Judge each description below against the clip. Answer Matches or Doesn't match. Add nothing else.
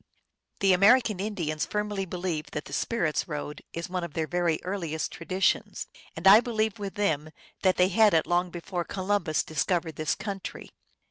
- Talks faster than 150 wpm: Matches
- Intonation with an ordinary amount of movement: Matches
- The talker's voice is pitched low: Doesn't match